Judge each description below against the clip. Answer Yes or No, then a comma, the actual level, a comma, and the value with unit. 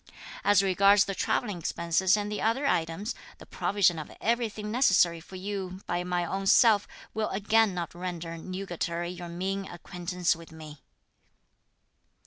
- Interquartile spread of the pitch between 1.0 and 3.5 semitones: Yes, average, 3.0 semitones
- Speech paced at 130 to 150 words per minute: Yes, average, 145 wpm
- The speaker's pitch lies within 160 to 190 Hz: Yes, medium, 185 Hz